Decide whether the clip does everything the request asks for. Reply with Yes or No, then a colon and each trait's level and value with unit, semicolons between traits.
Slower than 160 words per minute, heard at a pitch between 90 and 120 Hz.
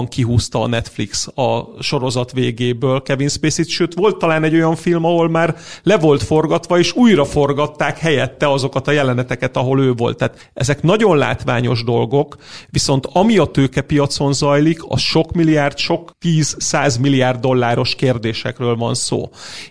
No: average, 150 wpm; medium, 140 Hz